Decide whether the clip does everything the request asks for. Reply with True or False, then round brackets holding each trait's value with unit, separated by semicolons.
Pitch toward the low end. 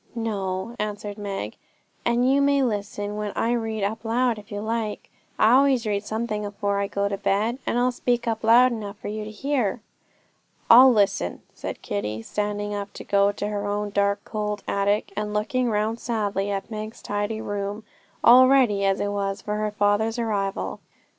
False (210 Hz)